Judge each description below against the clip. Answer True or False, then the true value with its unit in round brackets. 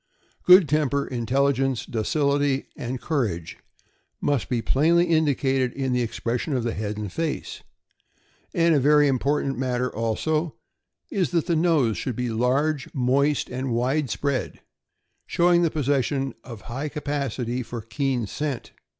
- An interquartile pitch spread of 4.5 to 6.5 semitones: False (3.4 semitones)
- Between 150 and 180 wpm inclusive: False (140 wpm)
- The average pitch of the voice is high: False (135 Hz)